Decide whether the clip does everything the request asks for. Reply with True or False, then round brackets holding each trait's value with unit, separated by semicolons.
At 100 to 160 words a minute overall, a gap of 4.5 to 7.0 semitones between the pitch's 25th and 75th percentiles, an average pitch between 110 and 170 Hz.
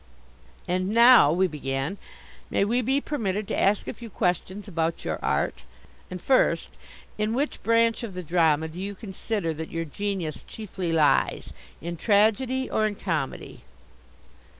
False (150 wpm; 5.0 semitones; 195 Hz)